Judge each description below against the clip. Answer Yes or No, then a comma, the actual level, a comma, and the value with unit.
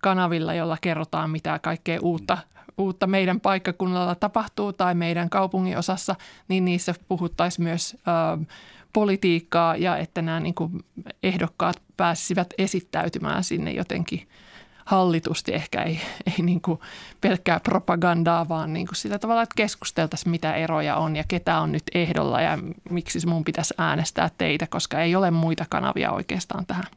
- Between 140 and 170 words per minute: Yes, average, 145 wpm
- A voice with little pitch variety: Yes, narrow, 2.1 semitones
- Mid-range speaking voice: Yes, medium, 175 Hz